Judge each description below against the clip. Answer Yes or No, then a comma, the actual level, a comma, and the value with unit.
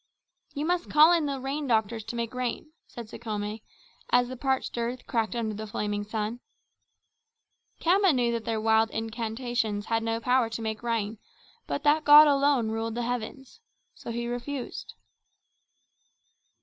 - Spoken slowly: No, average, 155 wpm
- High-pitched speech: Yes, high, 235 Hz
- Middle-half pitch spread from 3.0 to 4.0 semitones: Yes, average, 3.3 semitones